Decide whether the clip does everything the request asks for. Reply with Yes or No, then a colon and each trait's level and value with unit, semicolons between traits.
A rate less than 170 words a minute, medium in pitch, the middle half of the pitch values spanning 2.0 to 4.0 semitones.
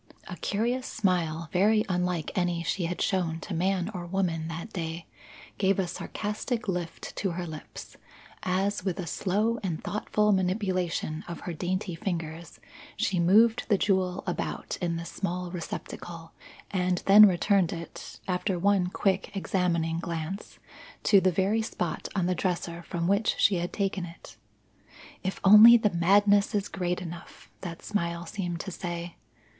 Yes: average, 155 wpm; medium, 180 Hz; narrow, 2.6 semitones